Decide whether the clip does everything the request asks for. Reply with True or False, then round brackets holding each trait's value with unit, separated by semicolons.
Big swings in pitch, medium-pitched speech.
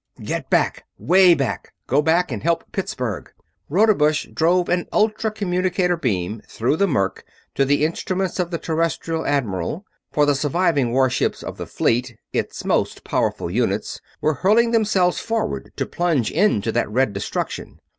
True (6.3 semitones; 160 Hz)